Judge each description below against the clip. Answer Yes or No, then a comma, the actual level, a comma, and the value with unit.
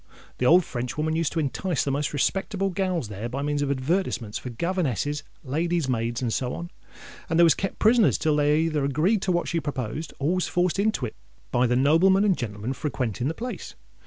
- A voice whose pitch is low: No, medium, 150 Hz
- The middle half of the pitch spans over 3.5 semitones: Yes, wide, 5.6 semitones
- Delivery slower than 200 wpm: No, fast, 205 wpm